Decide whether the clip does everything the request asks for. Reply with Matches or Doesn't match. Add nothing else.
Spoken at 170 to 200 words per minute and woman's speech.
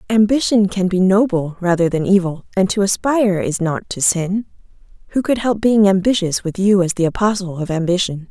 Matches